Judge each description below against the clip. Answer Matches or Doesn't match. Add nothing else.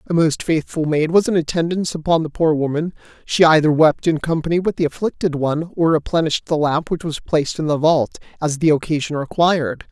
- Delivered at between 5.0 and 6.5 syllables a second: Matches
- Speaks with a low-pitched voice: Doesn't match